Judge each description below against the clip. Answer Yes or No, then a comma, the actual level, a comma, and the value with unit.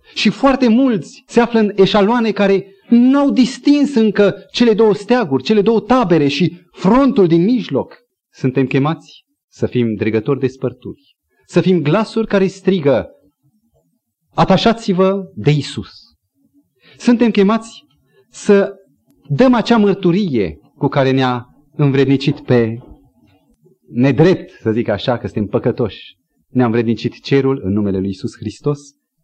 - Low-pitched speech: No, medium, 175 Hz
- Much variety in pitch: Yes, wide, 9.0 semitones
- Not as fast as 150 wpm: Yes, average, 130 wpm